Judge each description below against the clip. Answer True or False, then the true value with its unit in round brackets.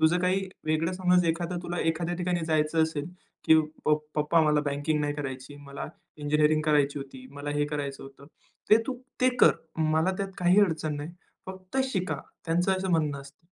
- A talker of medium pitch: True (155 Hz)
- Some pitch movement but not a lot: True (3.4 semitones)